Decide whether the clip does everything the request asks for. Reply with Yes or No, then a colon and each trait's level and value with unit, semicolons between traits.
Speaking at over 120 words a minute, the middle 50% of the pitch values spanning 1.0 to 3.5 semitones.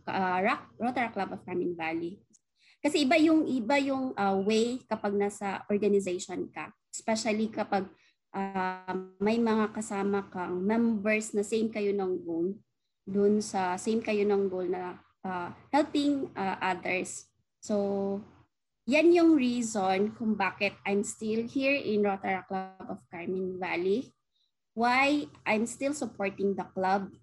Yes: average, 135 wpm; average, 3.2 semitones